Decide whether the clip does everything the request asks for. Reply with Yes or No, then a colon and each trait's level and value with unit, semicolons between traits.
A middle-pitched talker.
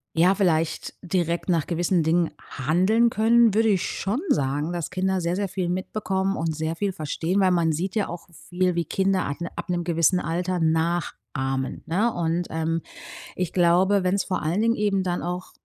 Yes: medium, 175 Hz